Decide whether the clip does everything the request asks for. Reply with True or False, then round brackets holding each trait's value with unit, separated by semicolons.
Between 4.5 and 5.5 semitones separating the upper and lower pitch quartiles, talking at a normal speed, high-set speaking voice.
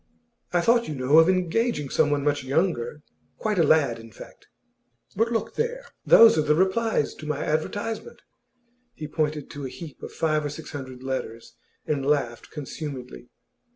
False (4.8 semitones; 165 wpm; 150 Hz)